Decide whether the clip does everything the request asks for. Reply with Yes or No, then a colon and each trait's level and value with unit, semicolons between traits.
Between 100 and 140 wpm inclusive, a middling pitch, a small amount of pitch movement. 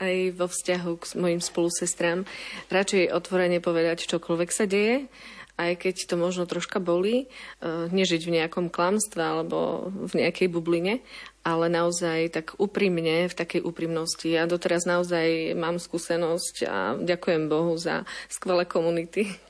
Yes: average, 135 wpm; medium, 175 Hz; narrow, 1.7 semitones